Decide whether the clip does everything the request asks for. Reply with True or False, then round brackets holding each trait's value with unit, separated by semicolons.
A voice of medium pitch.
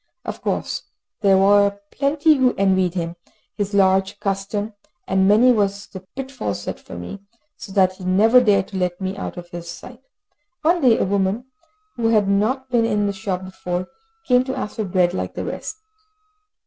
False (200 Hz)